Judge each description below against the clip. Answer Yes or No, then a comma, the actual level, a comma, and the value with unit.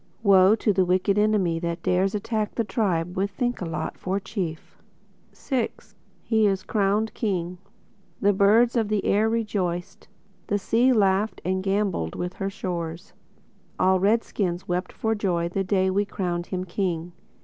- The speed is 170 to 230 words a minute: No, average, 155 wpm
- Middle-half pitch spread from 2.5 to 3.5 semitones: Yes, average, 2.9 semitones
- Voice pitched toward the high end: Yes, high, 195 Hz